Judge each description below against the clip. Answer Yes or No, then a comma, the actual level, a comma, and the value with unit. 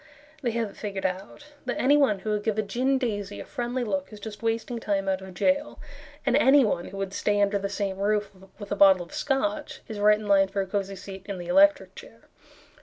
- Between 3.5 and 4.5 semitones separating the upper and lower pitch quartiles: Yes, average, 4.1 semitones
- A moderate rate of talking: No, fast, 230 wpm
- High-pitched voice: Yes, high, 210 Hz